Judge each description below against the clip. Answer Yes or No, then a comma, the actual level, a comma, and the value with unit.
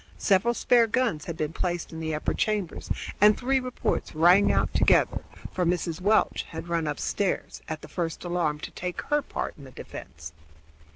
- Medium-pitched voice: Yes, medium, 175 Hz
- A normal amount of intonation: Yes, average, 4.8 semitones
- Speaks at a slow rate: No, average, 180 wpm